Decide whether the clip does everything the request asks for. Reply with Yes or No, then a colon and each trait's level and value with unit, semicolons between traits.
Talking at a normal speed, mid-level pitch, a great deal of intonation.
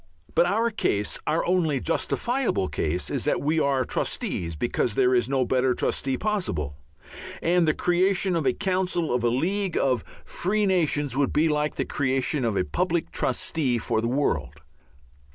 Yes: average, 170 wpm; medium, 145 Hz; wide, 6.2 semitones